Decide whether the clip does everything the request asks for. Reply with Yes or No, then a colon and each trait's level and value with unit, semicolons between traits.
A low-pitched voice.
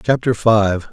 Yes: low, 110 Hz